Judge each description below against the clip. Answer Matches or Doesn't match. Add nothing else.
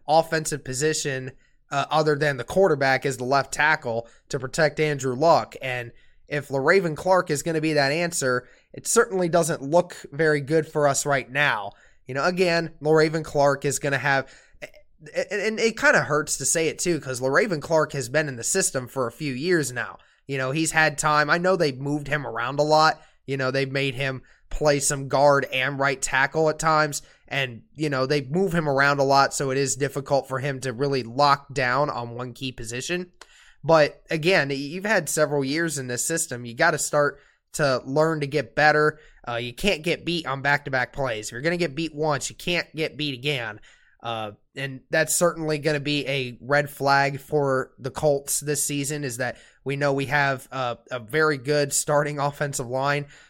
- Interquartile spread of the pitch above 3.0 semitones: Doesn't match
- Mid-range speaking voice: Matches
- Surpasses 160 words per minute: Matches